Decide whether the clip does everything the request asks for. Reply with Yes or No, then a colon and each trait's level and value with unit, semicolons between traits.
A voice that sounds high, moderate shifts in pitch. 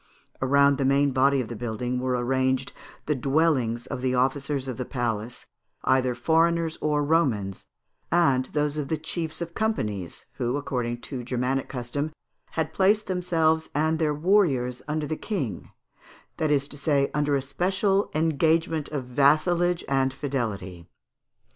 No: medium, 140 Hz; average, 4.0 semitones